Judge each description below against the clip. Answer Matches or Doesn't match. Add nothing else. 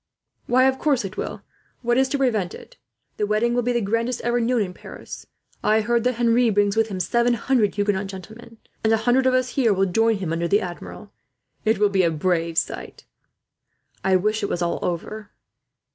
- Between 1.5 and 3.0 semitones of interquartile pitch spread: Doesn't match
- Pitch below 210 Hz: Doesn't match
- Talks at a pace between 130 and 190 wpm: Doesn't match